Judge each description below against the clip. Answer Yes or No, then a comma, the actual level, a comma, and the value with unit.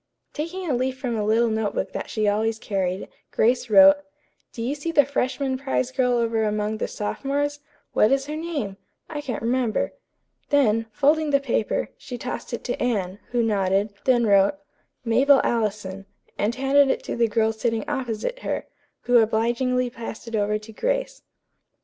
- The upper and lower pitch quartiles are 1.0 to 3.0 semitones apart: No, average, 4.1 semitones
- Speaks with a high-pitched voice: Yes, high, 235 Hz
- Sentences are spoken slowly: No, average, 175 wpm